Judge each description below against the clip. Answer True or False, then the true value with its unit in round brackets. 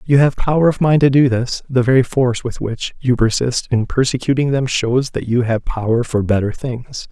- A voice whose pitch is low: True (125 Hz)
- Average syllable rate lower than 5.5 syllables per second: True (5.1 syllables/s)